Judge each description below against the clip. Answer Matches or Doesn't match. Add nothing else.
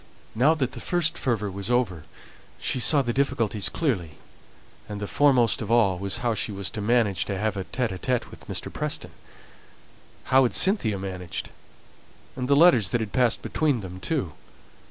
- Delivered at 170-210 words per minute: Matches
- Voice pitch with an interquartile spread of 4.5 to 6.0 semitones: Matches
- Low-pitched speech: Matches